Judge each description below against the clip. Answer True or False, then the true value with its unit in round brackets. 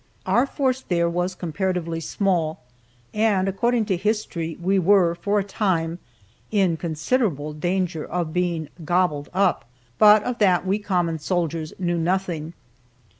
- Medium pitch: True (180 Hz)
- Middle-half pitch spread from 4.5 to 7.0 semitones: False (3.2 semitones)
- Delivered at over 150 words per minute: False (135 wpm)